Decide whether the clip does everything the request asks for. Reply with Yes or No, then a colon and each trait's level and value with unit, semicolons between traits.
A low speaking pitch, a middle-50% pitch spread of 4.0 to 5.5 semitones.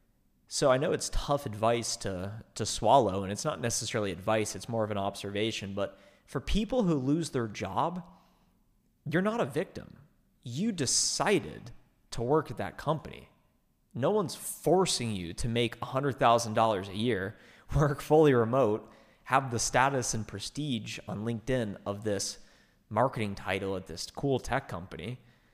Yes: low, 115 Hz; average, 5.0 semitones